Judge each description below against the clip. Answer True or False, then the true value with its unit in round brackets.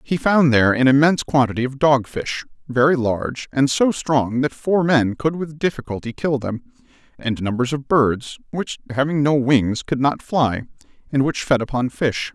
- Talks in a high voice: False (135 Hz)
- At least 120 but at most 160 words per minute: False (185 wpm)